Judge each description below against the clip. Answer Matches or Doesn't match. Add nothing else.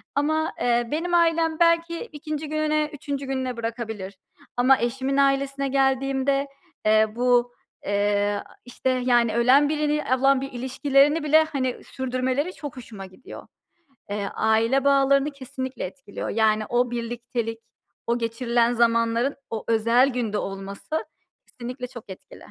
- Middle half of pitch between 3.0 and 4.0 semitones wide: Matches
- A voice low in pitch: Doesn't match